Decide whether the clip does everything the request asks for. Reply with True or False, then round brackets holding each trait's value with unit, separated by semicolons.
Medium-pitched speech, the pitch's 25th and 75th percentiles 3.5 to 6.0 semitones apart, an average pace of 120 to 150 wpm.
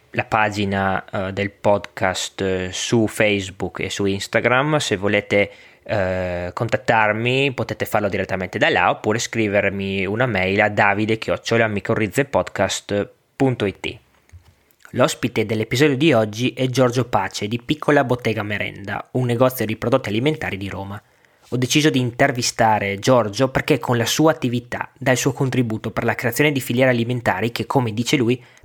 False (115 Hz; 4.0 semitones; 140 wpm)